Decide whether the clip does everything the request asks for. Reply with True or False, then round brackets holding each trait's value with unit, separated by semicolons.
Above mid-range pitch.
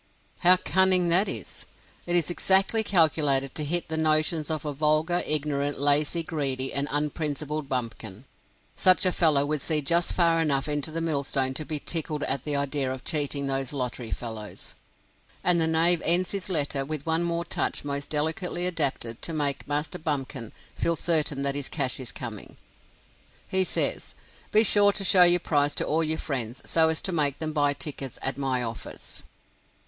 False (150 Hz)